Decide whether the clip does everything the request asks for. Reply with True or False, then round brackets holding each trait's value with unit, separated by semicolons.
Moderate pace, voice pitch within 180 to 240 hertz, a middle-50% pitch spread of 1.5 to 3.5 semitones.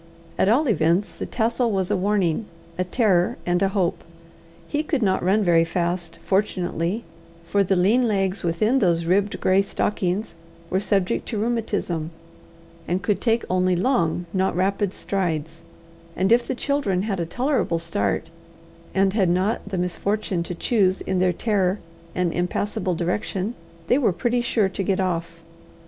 True (160 wpm; 190 Hz; 3.2 semitones)